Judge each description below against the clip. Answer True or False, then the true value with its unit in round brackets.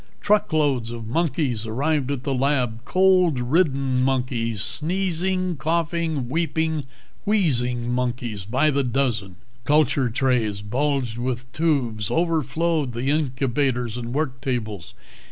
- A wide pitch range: False (4.6 semitones)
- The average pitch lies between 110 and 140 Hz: True (135 Hz)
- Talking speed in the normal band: False (115 wpm)